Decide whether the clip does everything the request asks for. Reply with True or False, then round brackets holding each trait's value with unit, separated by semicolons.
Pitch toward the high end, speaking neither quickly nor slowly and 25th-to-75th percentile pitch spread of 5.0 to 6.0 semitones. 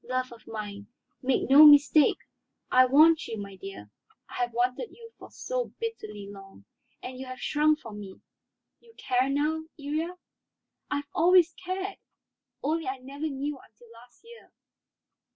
True (275 Hz; 150 wpm; 5.4 semitones)